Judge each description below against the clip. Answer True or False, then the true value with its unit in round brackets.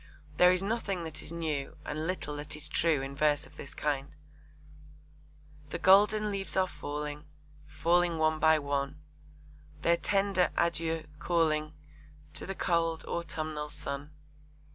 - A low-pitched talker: False (160 Hz)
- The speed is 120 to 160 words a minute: True (140 wpm)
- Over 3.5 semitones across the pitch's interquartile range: False (2.9 semitones)